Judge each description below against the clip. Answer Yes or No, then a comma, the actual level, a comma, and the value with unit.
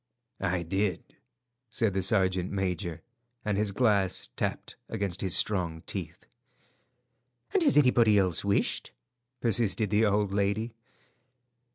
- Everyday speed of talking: No, slow, 115 wpm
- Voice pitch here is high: No, low, 100 Hz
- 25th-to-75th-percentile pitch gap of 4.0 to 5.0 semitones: No, narrow, 2.4 semitones